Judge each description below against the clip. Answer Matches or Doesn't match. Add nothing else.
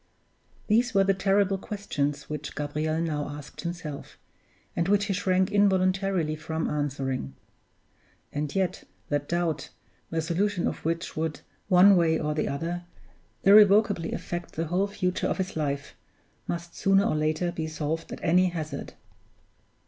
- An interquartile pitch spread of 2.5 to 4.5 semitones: Matches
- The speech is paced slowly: Doesn't match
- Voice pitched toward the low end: Doesn't match